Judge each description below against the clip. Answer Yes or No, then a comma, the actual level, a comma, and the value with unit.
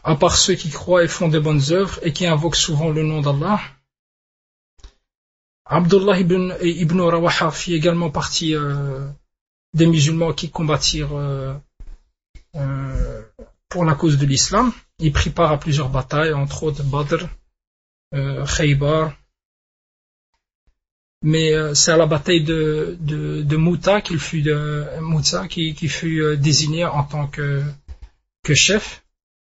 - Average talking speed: No, slow, 140 wpm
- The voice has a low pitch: No, medium, 155 Hz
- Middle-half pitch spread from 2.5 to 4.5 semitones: Yes, average, 2.9 semitones